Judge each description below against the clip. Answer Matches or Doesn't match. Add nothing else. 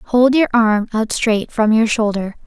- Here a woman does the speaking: Matches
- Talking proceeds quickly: Doesn't match